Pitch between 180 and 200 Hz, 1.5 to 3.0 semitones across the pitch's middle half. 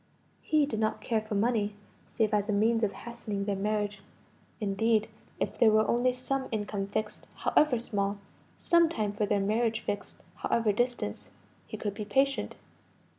No: high, 215 Hz; narrow, 2.5 semitones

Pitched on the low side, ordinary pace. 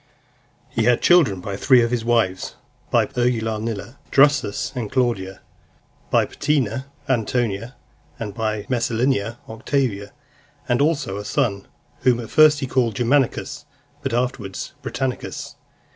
No: low, 120 Hz; slow, 130 wpm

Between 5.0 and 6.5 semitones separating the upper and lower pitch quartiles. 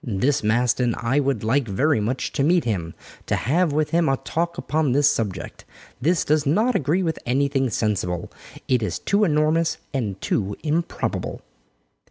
Yes: wide, 5.5 semitones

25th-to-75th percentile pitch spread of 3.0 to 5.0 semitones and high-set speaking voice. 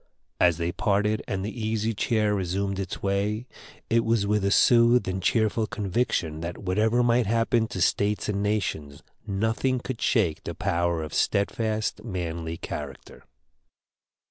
No: average, 3.4 semitones; low, 105 Hz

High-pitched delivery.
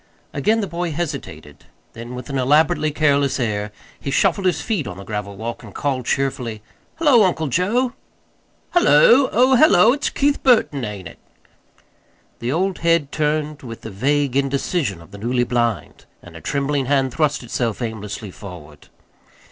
No: medium, 140 Hz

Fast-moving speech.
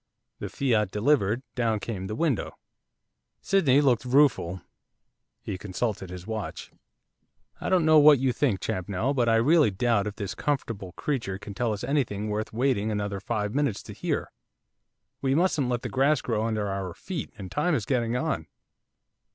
No: average, 165 wpm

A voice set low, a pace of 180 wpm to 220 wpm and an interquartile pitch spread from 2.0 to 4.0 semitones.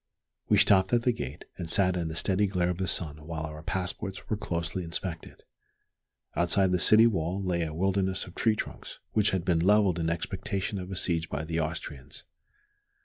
Yes: very low, 90 Hz; average, 195 wpm; average, 2.8 semitones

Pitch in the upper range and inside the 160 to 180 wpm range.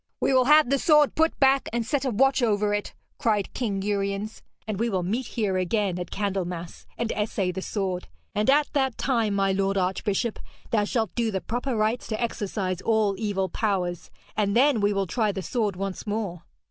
No: high, 210 Hz; average, 200 wpm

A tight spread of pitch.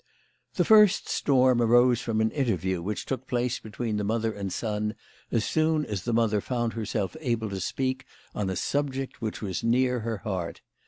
No: average, 3.4 semitones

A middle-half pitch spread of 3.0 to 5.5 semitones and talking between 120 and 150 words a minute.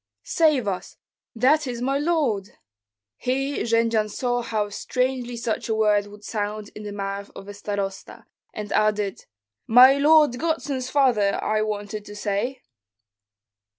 Yes: average, 3.9 semitones; average, 140 wpm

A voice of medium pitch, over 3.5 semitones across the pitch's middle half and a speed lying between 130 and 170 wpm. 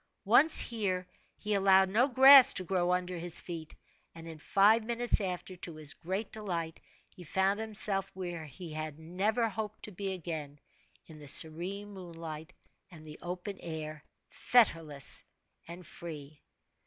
Yes: medium, 180 Hz; average, 4.0 semitones; average, 150 wpm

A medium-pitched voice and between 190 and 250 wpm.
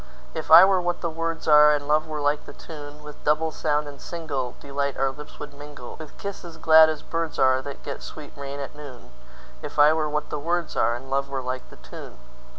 Yes: medium, 150 Hz; average, 195 wpm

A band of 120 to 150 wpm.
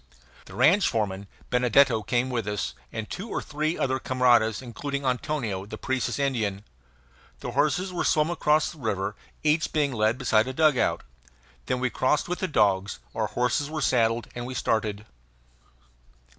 No: average, 160 wpm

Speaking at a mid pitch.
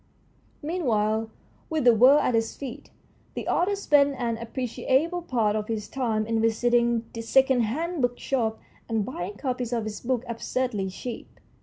No: high, 240 Hz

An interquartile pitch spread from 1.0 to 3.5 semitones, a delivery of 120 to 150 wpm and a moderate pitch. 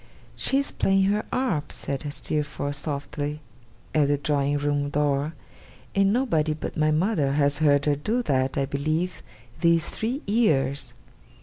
No: average, 4.3 semitones; average, 145 wpm; medium, 150 Hz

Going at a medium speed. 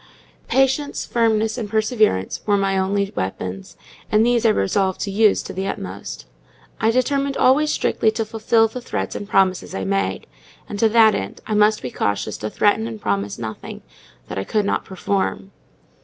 Yes: average, 175 wpm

